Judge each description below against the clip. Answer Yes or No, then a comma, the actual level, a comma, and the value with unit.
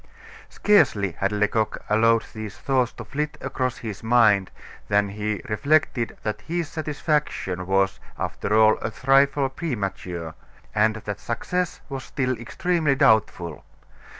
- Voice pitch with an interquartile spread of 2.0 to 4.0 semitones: No, average, 4.9 semitones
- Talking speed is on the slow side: Yes, slow, 125 wpm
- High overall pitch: No, low, 115 Hz